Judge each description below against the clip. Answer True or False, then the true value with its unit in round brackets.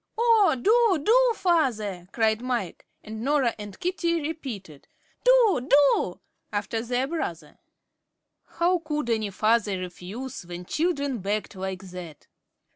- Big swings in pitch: True (8.6 semitones)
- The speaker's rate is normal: False (120 wpm)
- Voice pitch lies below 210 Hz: False (245 Hz)